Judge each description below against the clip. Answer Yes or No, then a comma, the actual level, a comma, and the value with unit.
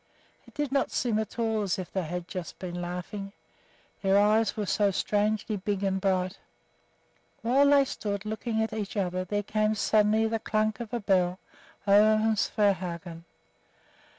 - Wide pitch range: No, narrow, 2.6 semitones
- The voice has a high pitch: Yes, high, 205 Hz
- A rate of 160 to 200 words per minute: Yes, average, 165 wpm